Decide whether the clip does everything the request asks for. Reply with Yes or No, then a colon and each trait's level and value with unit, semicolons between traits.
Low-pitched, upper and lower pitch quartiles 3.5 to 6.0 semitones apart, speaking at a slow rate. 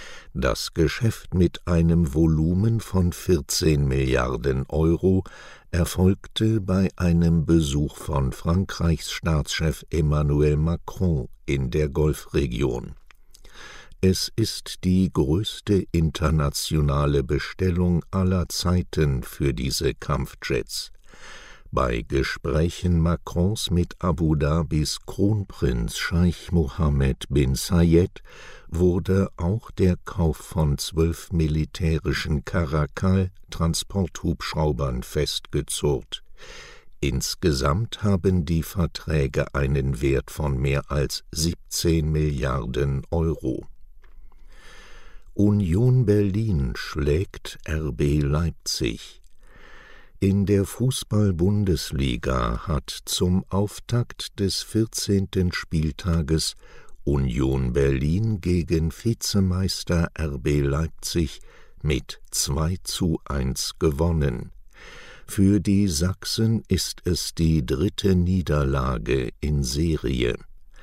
Yes: very low, 80 Hz; average, 4.2 semitones; slow, 85 wpm